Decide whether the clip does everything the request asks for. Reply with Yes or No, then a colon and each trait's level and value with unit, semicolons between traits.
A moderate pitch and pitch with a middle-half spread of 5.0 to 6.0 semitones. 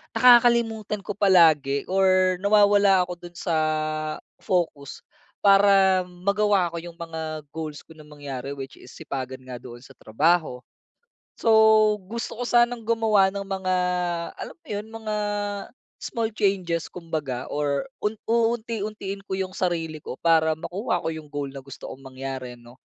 Yes: medium, 180 Hz; wide, 5.5 semitones